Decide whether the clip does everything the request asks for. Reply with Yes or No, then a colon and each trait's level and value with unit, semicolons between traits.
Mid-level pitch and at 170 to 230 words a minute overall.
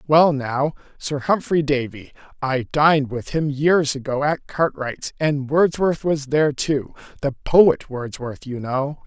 No: medium, 145 Hz; average, 145 wpm